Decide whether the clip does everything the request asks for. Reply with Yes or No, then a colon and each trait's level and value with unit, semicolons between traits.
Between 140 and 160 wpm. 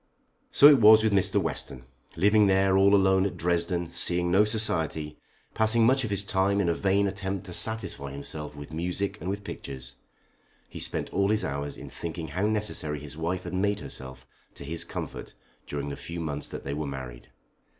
No: average, 190 wpm